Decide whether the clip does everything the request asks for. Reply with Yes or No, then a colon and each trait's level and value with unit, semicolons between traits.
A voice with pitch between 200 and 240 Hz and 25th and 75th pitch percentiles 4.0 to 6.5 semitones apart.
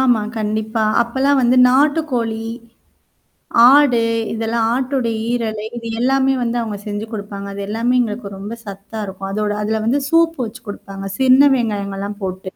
No: high, 225 Hz; average, 3.6 semitones